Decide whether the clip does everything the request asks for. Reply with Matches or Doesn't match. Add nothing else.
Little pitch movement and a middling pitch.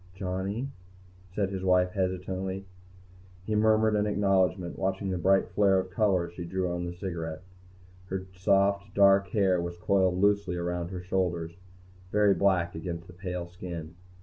Doesn't match